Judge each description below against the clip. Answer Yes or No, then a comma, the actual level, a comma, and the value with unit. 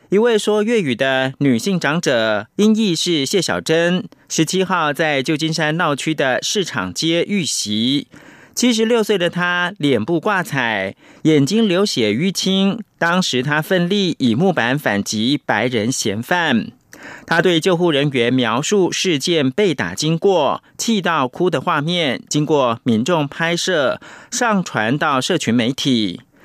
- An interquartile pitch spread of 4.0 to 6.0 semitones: Yes, wide, 5.6 semitones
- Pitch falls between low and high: Yes, medium, 170 Hz